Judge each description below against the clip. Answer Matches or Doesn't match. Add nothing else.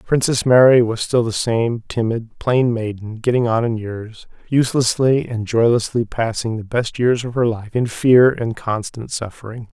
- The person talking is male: Matches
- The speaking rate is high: Doesn't match